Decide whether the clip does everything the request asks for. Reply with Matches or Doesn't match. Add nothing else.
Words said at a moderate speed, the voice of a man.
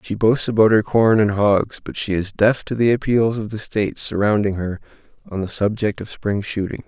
Doesn't match